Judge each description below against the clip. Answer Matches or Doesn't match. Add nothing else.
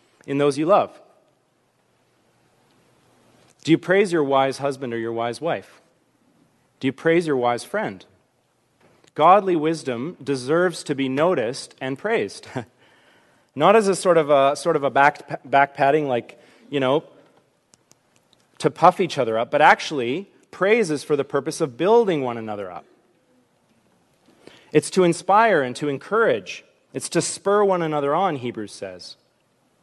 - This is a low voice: Doesn't match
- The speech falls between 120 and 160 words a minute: Matches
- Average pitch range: Matches